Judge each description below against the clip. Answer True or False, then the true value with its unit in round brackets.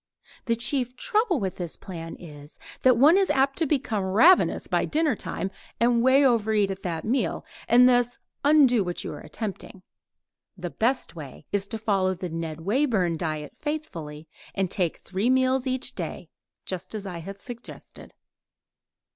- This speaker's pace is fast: False (160 wpm)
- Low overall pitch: False (215 Hz)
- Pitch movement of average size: False (6.3 semitones)